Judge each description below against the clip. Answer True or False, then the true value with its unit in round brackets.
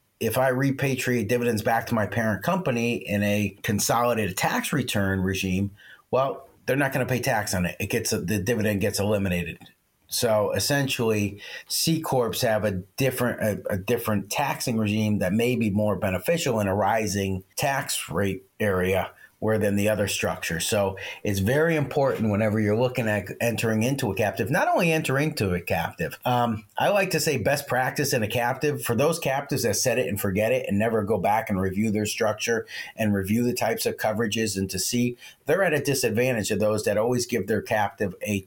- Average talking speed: True (195 wpm)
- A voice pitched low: True (110 Hz)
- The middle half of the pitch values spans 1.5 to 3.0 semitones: False (3.7 semitones)